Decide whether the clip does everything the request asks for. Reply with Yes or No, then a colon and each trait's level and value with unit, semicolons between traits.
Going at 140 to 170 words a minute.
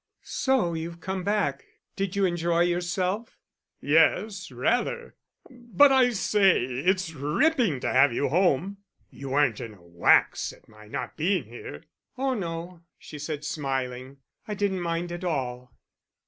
Yes: average, 145 wpm